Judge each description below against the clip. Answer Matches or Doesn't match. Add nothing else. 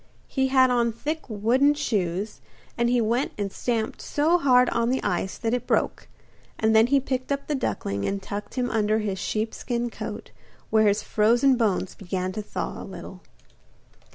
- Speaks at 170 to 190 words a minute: Matches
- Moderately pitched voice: Doesn't match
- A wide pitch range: Doesn't match